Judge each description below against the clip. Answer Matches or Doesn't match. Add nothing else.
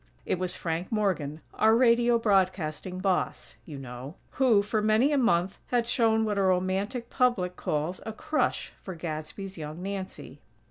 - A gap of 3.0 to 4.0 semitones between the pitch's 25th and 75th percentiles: Doesn't match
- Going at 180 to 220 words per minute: Doesn't match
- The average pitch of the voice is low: Doesn't match